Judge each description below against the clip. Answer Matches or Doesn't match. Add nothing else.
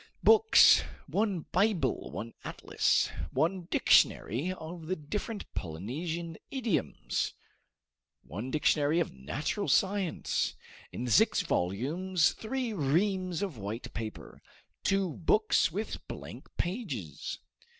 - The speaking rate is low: Matches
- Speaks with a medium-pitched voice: Matches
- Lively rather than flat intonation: Matches